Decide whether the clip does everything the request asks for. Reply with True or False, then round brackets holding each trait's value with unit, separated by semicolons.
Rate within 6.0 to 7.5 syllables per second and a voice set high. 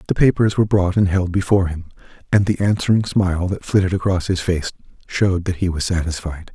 False (6.1 syllables/s; 95 Hz)